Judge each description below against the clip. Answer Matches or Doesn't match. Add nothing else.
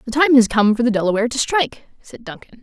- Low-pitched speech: Doesn't match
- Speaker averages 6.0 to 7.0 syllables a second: Matches